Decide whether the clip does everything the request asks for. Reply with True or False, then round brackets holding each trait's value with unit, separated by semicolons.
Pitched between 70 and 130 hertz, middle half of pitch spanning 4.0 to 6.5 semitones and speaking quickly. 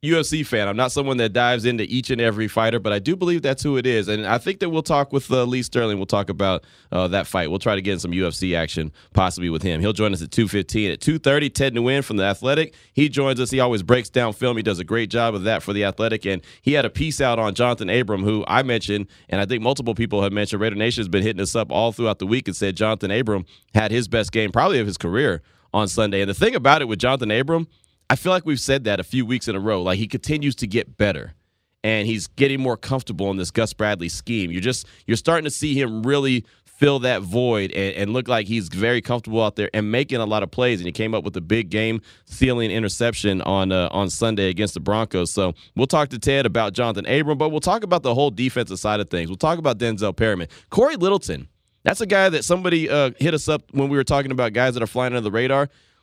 True (115 Hz; 4.4 semitones; 260 wpm)